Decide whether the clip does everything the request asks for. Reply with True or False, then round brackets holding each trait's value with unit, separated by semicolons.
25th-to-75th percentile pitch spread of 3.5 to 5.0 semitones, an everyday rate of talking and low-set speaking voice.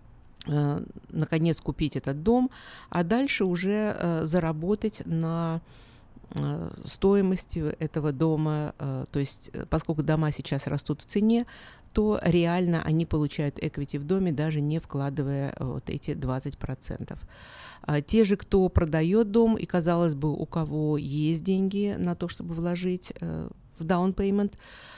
False (3.8 semitones; 125 wpm; 160 Hz)